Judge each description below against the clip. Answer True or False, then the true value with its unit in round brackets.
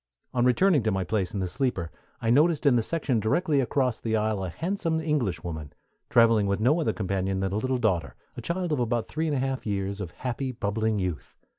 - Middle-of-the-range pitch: False (115 Hz)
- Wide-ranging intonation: True (5.8 semitones)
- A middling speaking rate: False (220 wpm)